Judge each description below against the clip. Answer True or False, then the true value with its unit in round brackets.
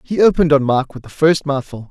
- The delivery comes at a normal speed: False (250 wpm)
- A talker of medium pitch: True (145 Hz)